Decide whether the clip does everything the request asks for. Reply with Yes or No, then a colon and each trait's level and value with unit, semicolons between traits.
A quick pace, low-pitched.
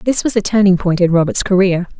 No: fast, 240 wpm; high, 190 Hz